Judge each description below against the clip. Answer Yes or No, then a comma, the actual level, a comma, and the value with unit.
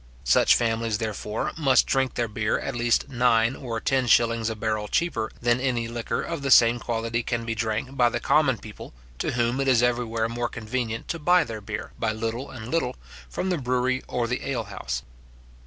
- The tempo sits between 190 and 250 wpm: Yes, average, 200 wpm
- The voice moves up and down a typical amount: No, narrow, 2.2 semitones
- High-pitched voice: No, low, 120 Hz